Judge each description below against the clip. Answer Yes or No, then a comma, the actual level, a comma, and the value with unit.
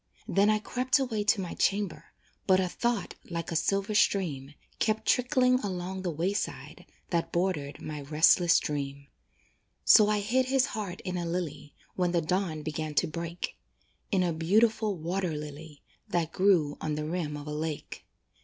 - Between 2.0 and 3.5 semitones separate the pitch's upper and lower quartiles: No, average, 4.7 semitones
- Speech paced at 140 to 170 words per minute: Yes, average, 165 wpm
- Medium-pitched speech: Yes, medium, 175 Hz